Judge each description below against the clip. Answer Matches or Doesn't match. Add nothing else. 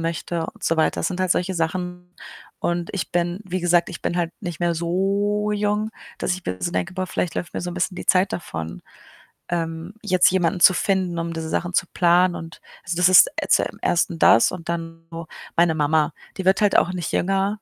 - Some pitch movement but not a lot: Doesn't match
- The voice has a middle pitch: Matches